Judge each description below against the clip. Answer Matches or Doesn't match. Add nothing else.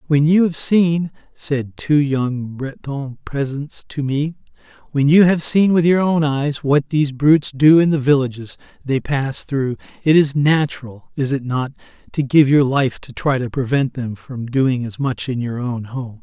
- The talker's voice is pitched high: Doesn't match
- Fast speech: Doesn't match